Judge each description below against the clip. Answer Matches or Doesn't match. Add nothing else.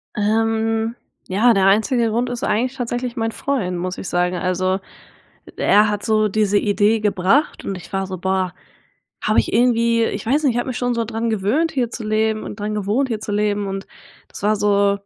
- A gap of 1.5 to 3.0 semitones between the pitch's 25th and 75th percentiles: Matches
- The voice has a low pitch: Doesn't match